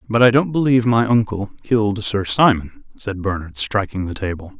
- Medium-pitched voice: No, low, 105 Hz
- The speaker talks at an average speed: Yes, average, 185 wpm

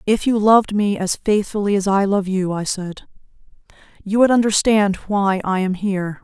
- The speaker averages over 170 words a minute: Yes, average, 185 wpm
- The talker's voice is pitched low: No, high, 200 Hz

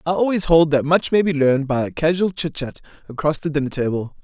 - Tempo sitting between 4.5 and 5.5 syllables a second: No, 5.8 syllables/s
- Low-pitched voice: No, medium, 155 Hz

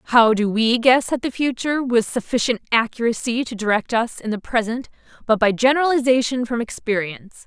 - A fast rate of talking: No, average, 170 wpm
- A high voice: Yes, high, 235 Hz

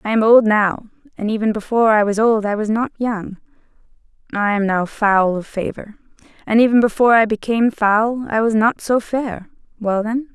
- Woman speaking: Yes, female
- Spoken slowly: No, average, 185 wpm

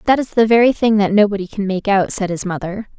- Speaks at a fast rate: Yes, fast, 260 wpm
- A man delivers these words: No, female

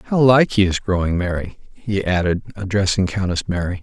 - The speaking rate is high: No, average, 175 wpm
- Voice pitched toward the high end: No, very low, 95 Hz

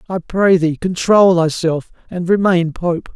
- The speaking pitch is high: No, medium, 175 Hz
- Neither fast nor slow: Yes, average, 150 wpm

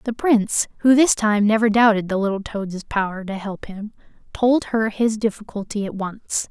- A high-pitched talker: Yes, high, 215 Hz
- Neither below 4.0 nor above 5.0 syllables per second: Yes, 4.8 syllables/s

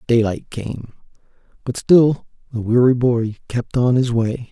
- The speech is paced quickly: No, average, 145 wpm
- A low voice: Yes, low, 120 Hz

